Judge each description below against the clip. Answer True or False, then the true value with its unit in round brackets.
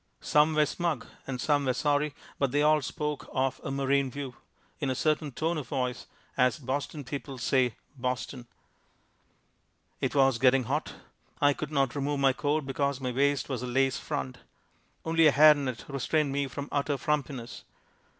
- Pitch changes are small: True (2.3 semitones)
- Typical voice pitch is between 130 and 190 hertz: True (140 Hz)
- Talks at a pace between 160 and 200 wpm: True (170 wpm)